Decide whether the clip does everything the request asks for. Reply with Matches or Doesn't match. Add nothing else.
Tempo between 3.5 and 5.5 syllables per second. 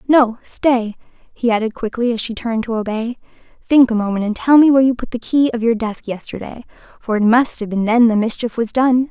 Doesn't match